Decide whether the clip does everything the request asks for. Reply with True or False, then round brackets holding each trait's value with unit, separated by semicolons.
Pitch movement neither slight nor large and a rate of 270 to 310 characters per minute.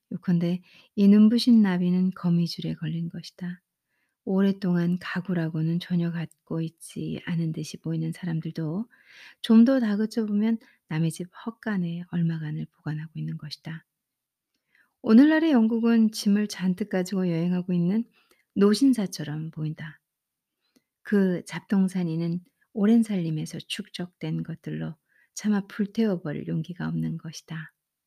True (4.2 semitones; 280 characters per minute)